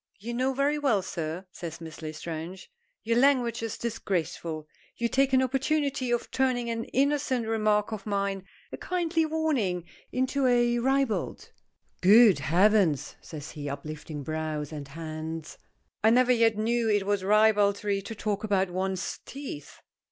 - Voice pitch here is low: No, high, 215 Hz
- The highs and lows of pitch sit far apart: Yes, wide, 6.3 semitones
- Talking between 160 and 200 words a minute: No, average, 150 wpm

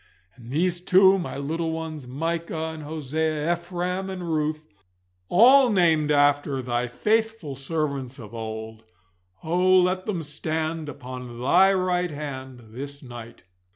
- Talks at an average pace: No, slow, 130 wpm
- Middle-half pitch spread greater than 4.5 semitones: Yes, average, 4.9 semitones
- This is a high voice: No, medium, 155 Hz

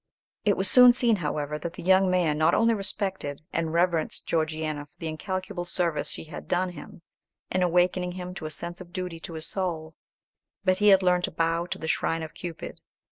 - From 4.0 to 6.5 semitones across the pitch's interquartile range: No, narrow, 2.6 semitones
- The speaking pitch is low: No, medium, 175 Hz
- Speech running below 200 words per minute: No, fast, 205 wpm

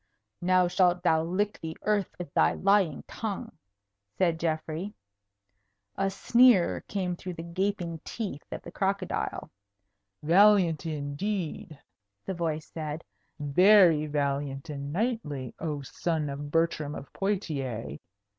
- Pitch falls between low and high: Yes, medium, 170 Hz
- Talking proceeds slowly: Yes, slow, 120 wpm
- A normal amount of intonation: Yes, average, 4.5 semitones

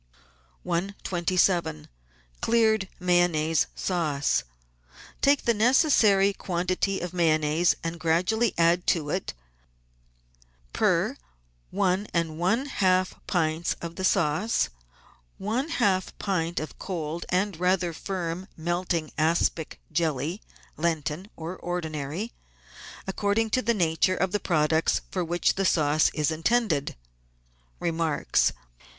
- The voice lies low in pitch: No, medium, 175 Hz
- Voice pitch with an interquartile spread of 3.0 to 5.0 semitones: Yes, average, 3.3 semitones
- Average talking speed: No, slow, 110 wpm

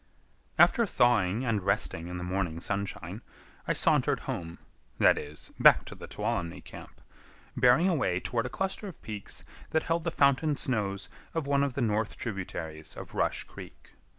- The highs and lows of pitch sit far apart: Yes, wide, 7.6 semitones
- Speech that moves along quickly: No, average, 155 wpm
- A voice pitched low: Yes, low, 110 Hz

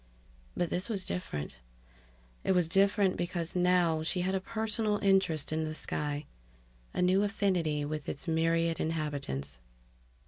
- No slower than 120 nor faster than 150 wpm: Yes, average, 140 wpm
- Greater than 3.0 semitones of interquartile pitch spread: Yes, average, 3.5 semitones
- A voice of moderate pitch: Yes, medium, 175 Hz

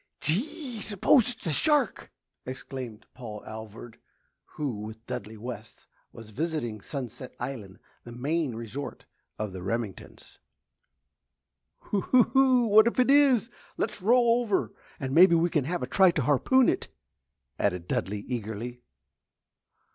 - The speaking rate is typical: No, slow, 130 wpm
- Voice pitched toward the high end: No, low, 135 Hz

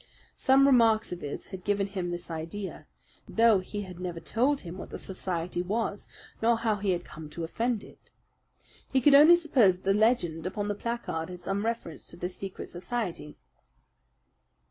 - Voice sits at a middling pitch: No, high, 195 Hz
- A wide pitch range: No, average, 4.6 semitones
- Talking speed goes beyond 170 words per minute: Yes, average, 180 wpm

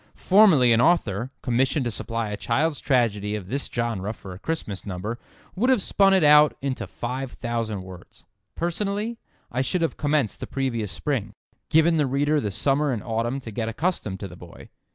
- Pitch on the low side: Yes, low, 125 Hz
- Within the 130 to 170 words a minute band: No, average, 180 wpm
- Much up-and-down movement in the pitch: Yes, wide, 5.9 semitones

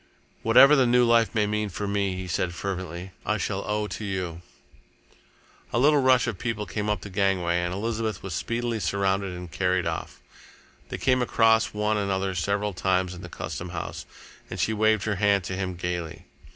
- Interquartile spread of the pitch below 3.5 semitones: Yes, average, 3.0 semitones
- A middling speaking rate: Yes, average, 190 wpm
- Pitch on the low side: Yes, low, 100 Hz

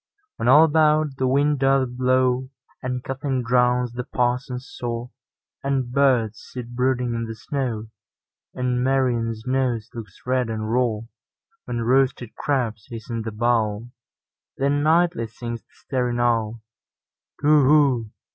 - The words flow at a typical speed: No, slow, 120 wpm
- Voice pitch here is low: Yes, low, 125 Hz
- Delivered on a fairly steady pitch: Yes, narrow, 2.3 semitones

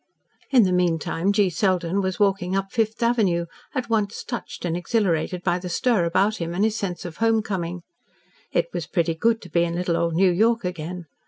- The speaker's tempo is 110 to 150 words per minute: No, average, 200 wpm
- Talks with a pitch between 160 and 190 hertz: Yes, medium, 185 Hz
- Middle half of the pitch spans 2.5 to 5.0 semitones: Yes, average, 3.8 semitones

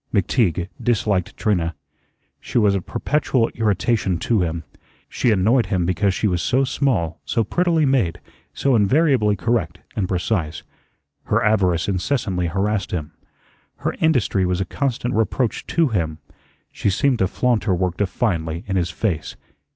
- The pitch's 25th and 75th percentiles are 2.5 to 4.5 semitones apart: No, average, 5.1 semitones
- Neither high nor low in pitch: No, low, 100 Hz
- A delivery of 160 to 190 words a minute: No, average, 150 wpm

